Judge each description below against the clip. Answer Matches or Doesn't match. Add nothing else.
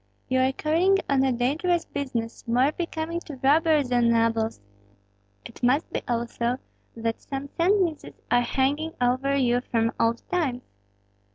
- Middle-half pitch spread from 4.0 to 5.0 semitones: Matches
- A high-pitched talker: Matches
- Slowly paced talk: Doesn't match